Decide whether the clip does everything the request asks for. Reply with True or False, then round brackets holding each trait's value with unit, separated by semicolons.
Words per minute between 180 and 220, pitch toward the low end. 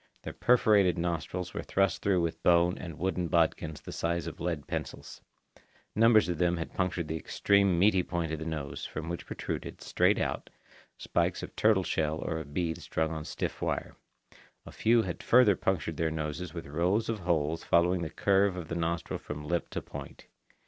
True (190 wpm; 85 Hz)